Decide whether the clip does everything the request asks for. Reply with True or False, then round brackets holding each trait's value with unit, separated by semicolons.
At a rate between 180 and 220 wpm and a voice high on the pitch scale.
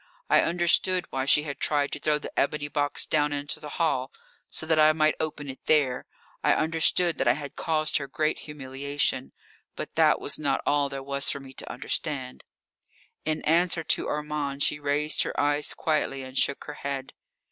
False (190 wpm; 145 Hz)